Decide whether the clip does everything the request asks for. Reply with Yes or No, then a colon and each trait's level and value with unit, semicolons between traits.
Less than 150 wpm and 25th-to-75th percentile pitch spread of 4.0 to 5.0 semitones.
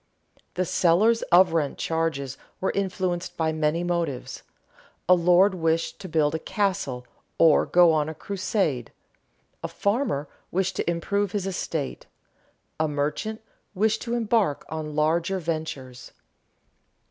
No: slow, 135 wpm; average, 3.6 semitones